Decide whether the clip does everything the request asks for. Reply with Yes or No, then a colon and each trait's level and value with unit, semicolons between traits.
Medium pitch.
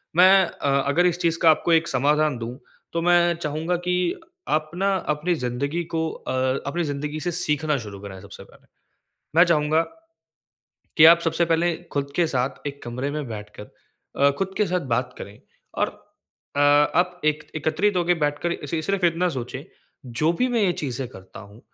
Yes: medium, 155 Hz